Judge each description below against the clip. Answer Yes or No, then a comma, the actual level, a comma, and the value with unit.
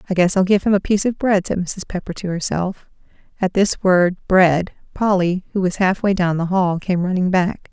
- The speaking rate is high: Yes, fast, 225 wpm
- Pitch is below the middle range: No, medium, 185 Hz